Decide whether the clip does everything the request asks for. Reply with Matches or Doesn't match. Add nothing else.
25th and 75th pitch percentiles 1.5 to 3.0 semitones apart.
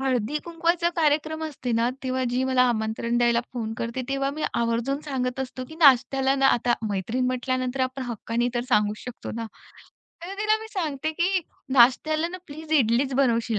Doesn't match